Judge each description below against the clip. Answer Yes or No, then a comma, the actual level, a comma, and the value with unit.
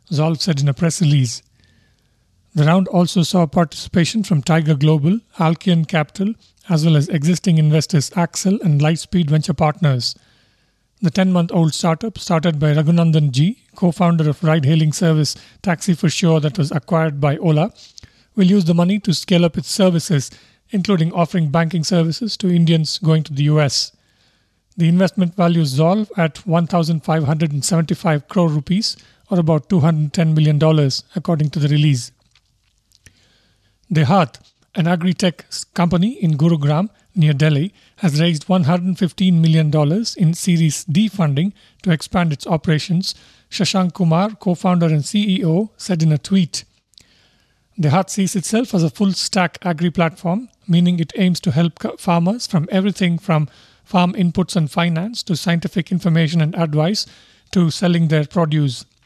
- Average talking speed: Yes, average, 150 wpm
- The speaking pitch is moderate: Yes, medium, 165 Hz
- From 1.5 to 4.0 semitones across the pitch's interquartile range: Yes, average, 2.8 semitones